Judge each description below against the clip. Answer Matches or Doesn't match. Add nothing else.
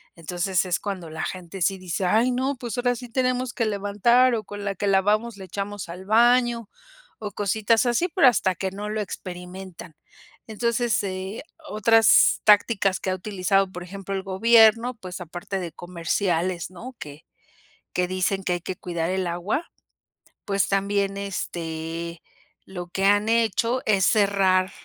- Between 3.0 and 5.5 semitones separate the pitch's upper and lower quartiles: Matches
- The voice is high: Matches